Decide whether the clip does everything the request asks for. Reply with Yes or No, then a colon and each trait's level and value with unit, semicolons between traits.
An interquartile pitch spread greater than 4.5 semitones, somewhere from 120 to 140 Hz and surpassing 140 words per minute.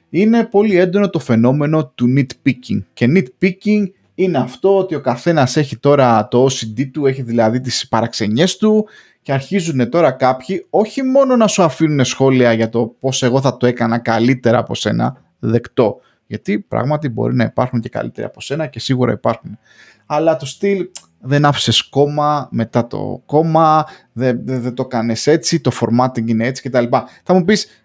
Yes: average, 5.3 semitones; low, 130 Hz; fast, 170 wpm